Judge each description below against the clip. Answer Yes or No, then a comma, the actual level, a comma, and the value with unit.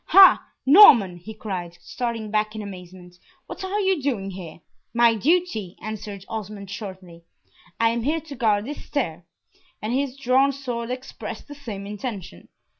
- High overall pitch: Yes, high, 220 Hz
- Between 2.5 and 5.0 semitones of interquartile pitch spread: No, wide, 5.5 semitones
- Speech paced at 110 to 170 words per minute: Yes, average, 155 wpm